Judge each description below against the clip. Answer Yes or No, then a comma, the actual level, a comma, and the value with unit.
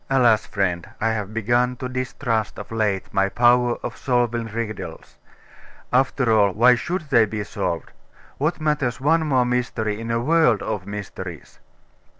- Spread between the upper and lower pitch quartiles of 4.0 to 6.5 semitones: No, average, 3.1 semitones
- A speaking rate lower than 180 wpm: Yes, average, 150 wpm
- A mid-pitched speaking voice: No, low, 115 Hz